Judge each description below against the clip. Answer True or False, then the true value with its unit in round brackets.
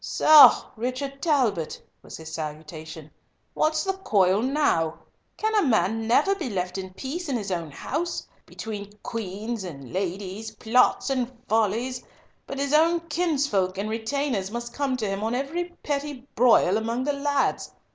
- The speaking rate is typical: True (155 wpm)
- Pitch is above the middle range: True (235 Hz)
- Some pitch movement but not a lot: False (6.6 semitones)